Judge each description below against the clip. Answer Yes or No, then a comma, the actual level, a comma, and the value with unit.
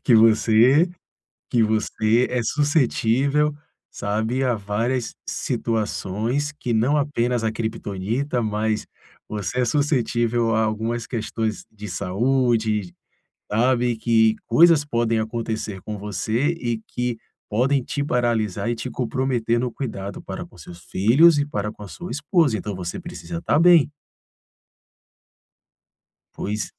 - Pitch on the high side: No, low, 115 Hz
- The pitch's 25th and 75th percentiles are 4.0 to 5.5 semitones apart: No, average, 3.4 semitones